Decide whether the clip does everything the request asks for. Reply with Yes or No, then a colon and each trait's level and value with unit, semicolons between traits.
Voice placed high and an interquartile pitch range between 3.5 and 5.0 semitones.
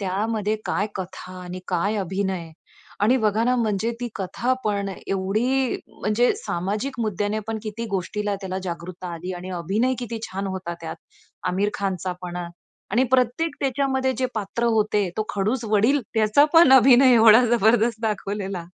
Yes: high, 210 Hz; average, 4.0 semitones